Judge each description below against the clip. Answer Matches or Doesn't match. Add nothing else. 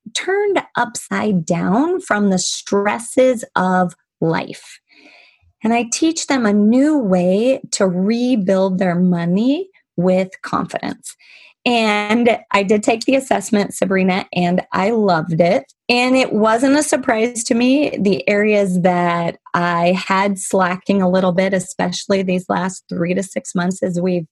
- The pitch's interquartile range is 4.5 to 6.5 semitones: Matches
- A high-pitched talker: Matches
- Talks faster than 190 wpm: Doesn't match